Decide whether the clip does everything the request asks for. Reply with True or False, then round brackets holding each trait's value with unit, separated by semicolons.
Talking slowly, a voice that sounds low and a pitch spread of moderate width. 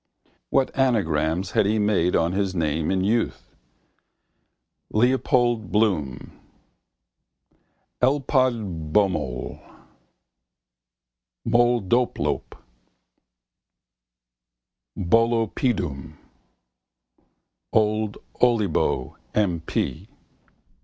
False (55 wpm; 105 Hz; 5.9 semitones)